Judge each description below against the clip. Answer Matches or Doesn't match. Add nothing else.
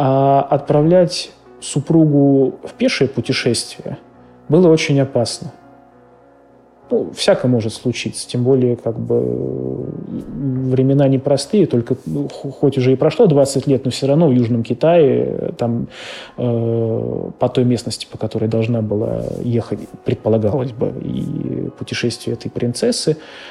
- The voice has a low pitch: Matches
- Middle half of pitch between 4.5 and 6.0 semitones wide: Doesn't match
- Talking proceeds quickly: Doesn't match